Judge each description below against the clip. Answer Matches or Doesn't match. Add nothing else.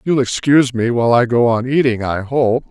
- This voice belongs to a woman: Doesn't match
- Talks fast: Matches